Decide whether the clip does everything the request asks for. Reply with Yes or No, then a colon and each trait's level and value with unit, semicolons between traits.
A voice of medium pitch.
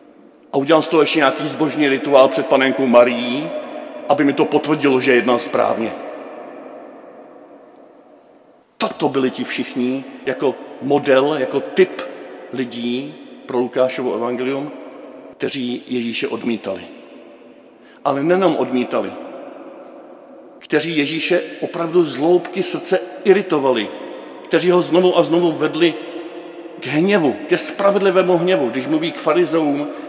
Yes: medium, 155 Hz